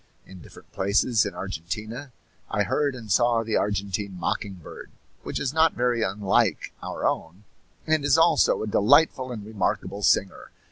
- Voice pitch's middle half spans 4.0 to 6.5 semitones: Yes, average, 4.3 semitones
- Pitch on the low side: Yes, low, 110 Hz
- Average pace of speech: Yes, average, 155 wpm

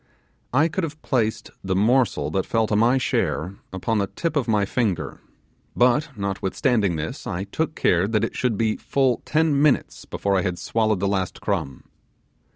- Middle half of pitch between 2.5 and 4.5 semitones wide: No, average, 5.0 semitones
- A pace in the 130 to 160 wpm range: No, average, 175 wpm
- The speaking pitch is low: Yes, low, 110 Hz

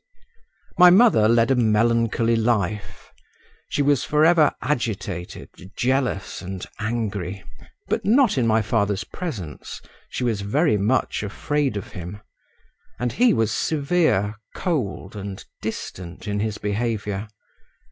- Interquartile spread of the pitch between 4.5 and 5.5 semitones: Yes, average, 5.1 semitones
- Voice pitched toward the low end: Yes, low, 110 Hz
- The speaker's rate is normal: No, slow, 125 wpm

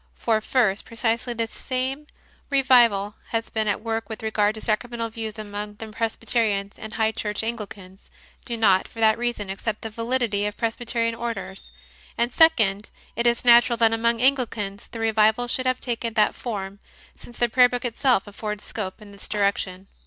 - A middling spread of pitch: No, narrow, 2.3 semitones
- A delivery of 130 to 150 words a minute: No, average, 175 wpm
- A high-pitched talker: Yes, high, 225 Hz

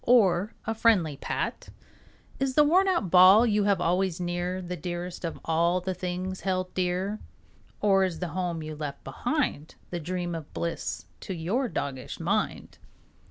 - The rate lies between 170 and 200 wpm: No, average, 160 wpm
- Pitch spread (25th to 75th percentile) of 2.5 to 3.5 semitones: Yes, average, 2.8 semitones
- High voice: No, medium, 180 Hz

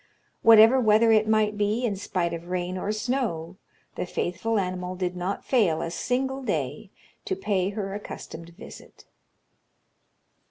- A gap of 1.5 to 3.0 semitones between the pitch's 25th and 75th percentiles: No, average, 3.8 semitones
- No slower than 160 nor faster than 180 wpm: No, average, 145 wpm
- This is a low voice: No, high, 205 Hz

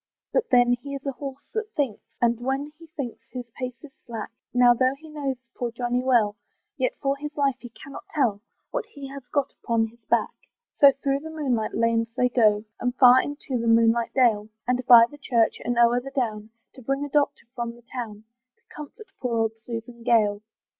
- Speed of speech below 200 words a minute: No, fast, 205 wpm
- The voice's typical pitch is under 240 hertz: No, very high, 250 Hz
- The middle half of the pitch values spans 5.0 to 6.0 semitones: No, average, 3.1 semitones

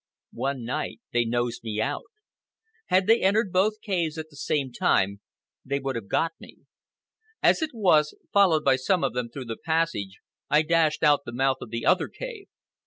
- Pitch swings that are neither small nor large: No, wide, 7.2 semitones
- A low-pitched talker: No, medium, 150 Hz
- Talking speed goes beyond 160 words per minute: Yes, average, 185 wpm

